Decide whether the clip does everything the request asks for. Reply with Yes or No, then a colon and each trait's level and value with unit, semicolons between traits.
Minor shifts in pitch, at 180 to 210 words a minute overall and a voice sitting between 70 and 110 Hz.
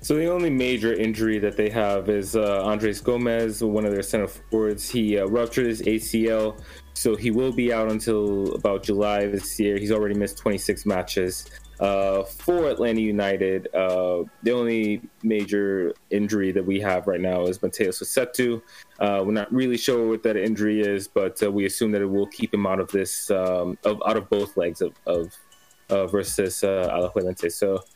Yes: narrow, 2.3 semitones; average, 190 wpm; low, 105 Hz